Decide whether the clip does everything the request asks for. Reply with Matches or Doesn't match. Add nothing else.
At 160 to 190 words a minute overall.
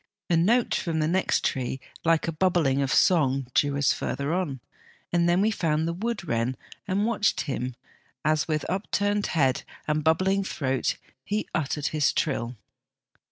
Matches